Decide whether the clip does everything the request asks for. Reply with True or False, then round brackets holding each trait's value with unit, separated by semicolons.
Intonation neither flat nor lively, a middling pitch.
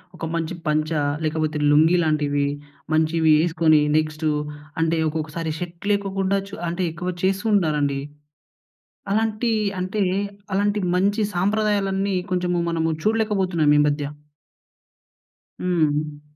True (3.9 semitones; 170 Hz)